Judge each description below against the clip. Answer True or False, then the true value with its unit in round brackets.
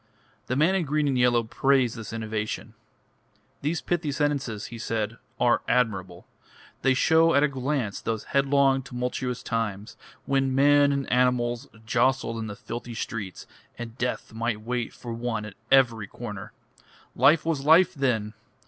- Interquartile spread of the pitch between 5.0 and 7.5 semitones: False (3.5 semitones)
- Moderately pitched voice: False (125 Hz)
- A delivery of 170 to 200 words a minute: False (150 wpm)